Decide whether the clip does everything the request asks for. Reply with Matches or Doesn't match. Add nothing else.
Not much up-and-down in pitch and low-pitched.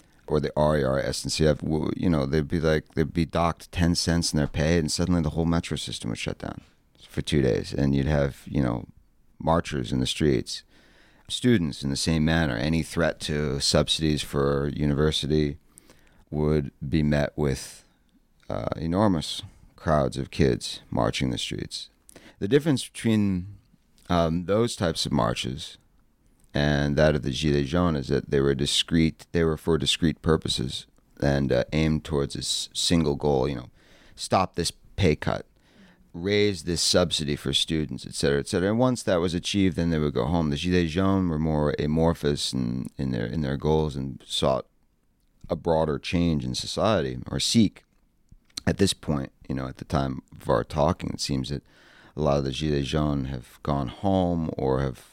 Doesn't match